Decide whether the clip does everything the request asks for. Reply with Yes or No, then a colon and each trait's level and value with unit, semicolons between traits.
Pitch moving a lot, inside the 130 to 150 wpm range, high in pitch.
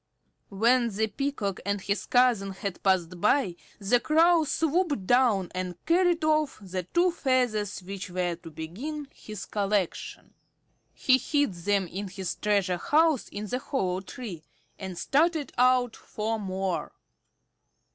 Yes: wide, 6.4 semitones; slow, 135 wpm; high, 210 Hz